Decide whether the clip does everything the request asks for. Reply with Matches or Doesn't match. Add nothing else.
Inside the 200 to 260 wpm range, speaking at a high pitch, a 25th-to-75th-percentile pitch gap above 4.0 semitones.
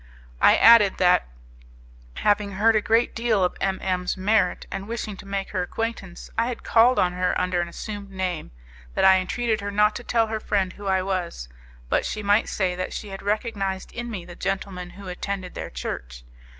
Doesn't match